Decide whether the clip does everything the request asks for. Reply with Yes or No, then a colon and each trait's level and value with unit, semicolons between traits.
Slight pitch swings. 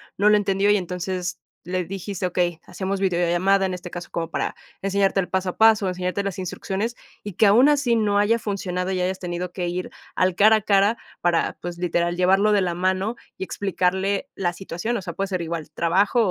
Yes: narrow, 2.2 semitones